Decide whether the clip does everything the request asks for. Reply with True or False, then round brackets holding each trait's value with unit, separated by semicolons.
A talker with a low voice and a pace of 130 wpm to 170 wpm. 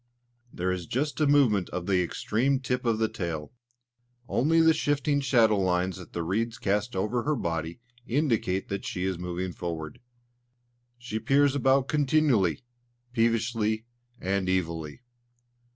True (110 Hz; 140 wpm)